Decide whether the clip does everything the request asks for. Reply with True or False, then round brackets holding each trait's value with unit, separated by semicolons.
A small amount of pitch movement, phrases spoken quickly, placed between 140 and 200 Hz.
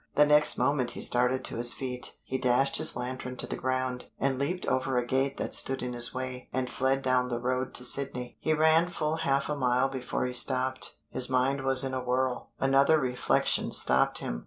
False (1.4 semitones; 210 wpm; 130 Hz)